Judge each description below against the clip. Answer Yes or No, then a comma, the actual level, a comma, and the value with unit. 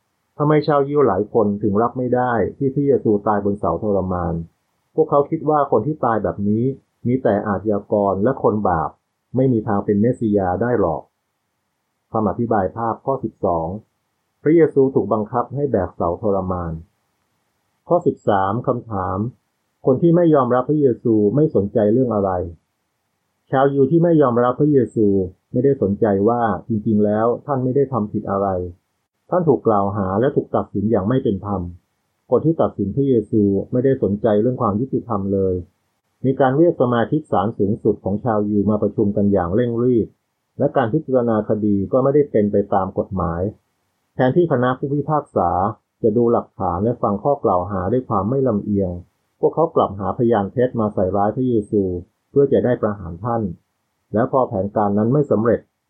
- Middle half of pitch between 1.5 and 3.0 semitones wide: No, average, 4.4 semitones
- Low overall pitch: Yes, low, 110 Hz